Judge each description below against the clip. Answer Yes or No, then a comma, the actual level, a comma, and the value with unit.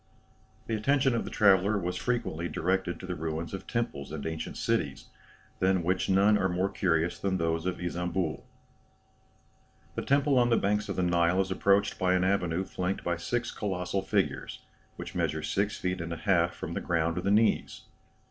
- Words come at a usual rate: Yes, average, 185 wpm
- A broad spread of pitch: No, narrow, 2.6 semitones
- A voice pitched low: Yes, very low, 95 Hz